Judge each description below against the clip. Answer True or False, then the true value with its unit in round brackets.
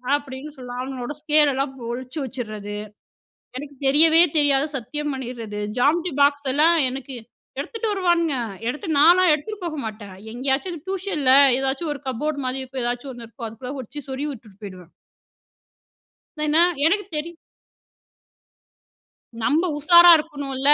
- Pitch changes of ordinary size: True (3.6 semitones)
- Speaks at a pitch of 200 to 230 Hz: False (280 Hz)